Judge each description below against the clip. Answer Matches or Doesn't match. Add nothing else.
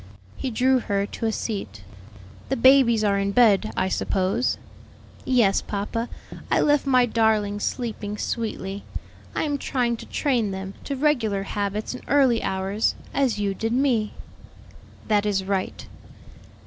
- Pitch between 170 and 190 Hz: Doesn't match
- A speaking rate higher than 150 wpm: Doesn't match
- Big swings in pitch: Doesn't match